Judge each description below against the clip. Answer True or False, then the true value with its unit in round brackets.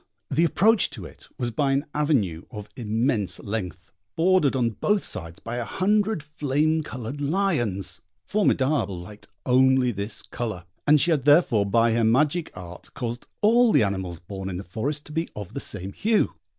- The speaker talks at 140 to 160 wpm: False (175 wpm)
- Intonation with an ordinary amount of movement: False (6.9 semitones)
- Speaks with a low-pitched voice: True (125 Hz)